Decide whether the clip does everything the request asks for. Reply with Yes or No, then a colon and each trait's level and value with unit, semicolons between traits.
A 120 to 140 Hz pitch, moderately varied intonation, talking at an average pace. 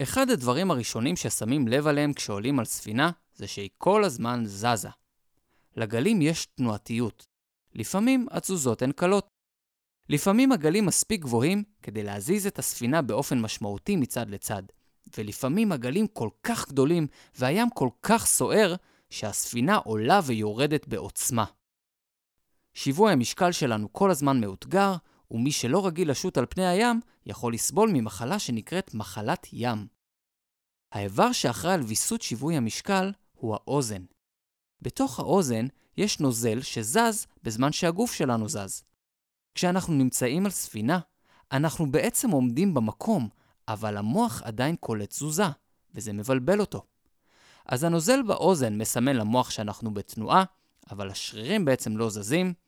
No: low, 135 Hz; wide, 8.9 semitones; average, 125 wpm